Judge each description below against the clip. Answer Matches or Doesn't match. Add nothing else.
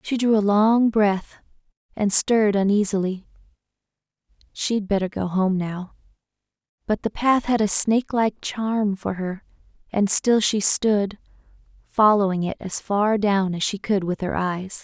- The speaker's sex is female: Matches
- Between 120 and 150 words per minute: Matches